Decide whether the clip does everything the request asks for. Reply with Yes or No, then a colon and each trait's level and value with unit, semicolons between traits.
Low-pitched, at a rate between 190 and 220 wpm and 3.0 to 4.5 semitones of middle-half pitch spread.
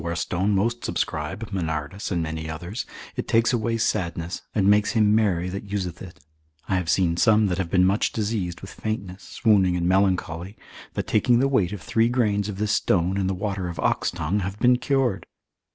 Yes: very low, 95 Hz; average, 200 wpm; average, 3.5 semitones